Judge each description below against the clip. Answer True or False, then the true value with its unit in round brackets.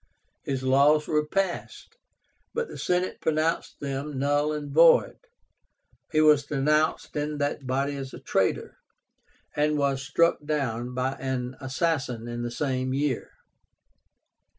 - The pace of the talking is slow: True (130 wpm)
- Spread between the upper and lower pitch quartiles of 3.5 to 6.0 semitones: False (2.5 semitones)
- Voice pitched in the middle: True (145 Hz)